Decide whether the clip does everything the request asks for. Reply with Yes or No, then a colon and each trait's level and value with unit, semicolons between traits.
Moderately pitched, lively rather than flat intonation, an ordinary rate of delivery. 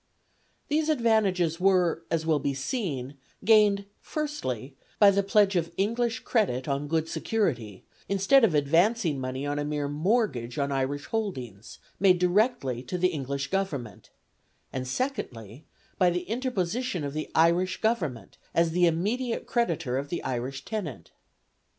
Yes: medium, 170 Hz; wide, 7.1 semitones; average, 145 wpm